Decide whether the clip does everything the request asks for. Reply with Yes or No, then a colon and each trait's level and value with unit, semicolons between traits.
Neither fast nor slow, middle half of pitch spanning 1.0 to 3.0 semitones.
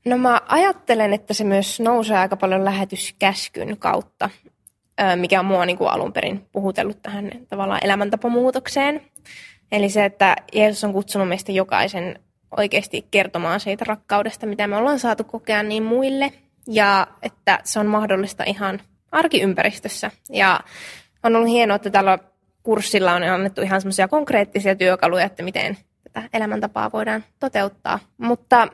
Yes: average, 140 wpm; narrow, 2.6 semitones